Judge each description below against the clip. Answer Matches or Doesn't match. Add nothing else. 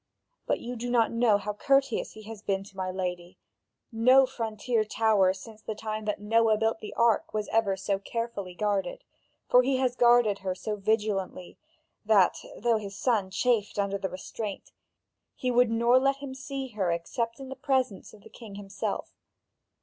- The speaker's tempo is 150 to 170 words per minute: Doesn't match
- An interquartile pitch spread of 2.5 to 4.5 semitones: Matches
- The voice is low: Doesn't match